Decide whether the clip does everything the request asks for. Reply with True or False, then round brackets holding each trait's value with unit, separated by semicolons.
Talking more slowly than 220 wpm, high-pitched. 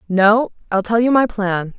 True (200 wpm; 210 Hz)